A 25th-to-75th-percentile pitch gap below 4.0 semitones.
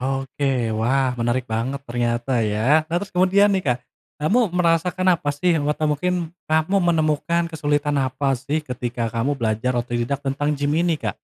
No: average, 4.9 semitones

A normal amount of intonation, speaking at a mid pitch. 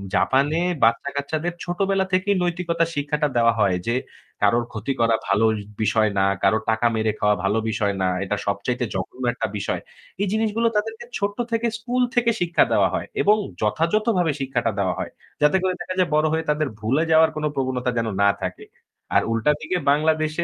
No: wide, 8.0 semitones; medium, 150 Hz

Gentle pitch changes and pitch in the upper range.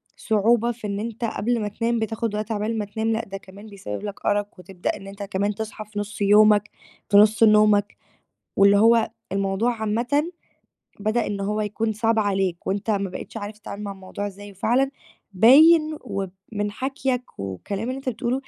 Yes: narrow, 2.2 semitones; high, 210 Hz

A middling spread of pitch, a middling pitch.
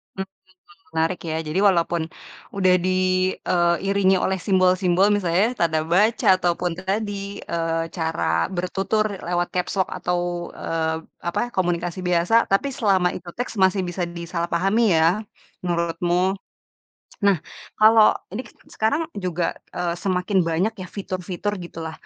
No: narrow, 2.3 semitones; medium, 180 Hz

